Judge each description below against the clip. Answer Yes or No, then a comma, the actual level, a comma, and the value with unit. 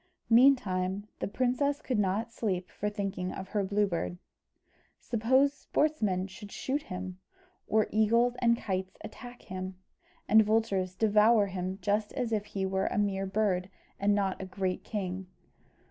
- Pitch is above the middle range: Yes, high, 205 Hz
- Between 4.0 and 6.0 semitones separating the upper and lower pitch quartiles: No, average, 3.2 semitones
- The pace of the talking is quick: No, average, 150 wpm